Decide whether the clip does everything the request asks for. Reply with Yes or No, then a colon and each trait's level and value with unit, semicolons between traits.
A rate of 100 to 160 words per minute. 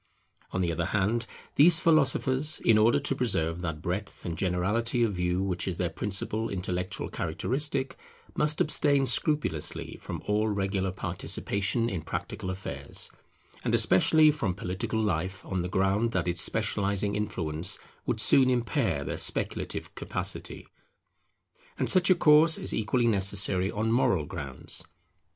Yes: average, 140 wpm